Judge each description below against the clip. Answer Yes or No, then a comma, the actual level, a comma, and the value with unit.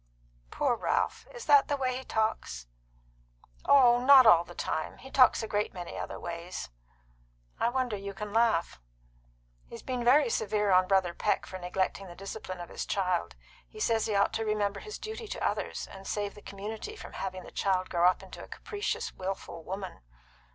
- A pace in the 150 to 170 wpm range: No, average, 185 wpm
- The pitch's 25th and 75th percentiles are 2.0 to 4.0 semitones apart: No, average, 4.7 semitones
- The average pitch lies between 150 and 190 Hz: No, high, 205 Hz